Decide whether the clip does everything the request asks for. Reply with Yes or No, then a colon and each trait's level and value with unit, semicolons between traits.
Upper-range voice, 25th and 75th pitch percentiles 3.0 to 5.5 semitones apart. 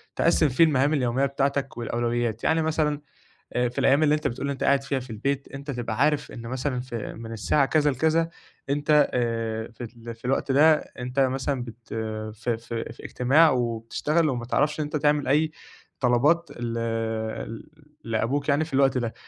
No: low, 135 Hz; average, 3.8 semitones